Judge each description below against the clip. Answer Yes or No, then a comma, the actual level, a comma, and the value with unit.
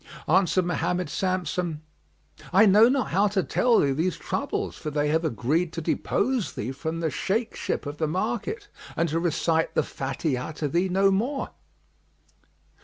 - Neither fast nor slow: Yes, average, 165 wpm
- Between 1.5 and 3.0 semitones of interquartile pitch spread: No, average, 4.0 semitones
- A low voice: No, medium, 175 Hz